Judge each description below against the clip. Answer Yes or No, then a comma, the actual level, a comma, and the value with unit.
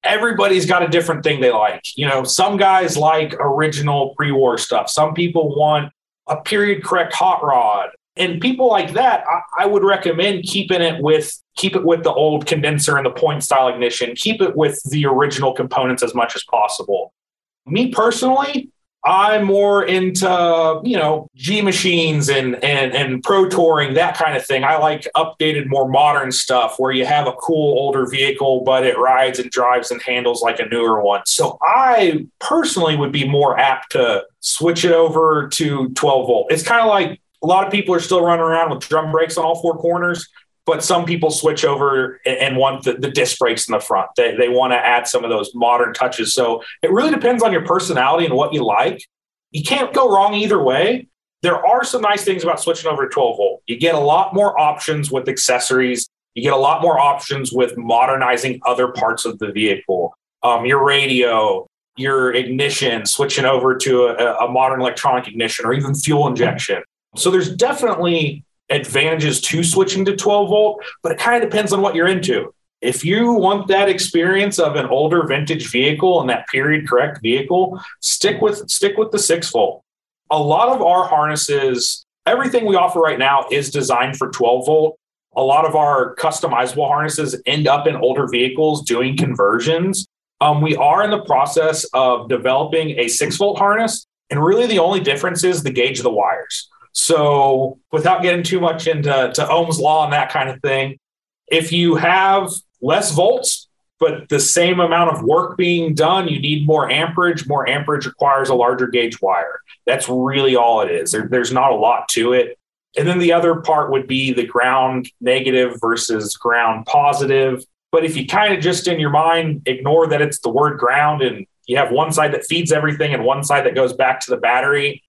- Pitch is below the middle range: No, medium, 155 Hz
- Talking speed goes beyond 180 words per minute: Yes, average, 195 wpm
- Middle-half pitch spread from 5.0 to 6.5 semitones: Yes, average, 5.3 semitones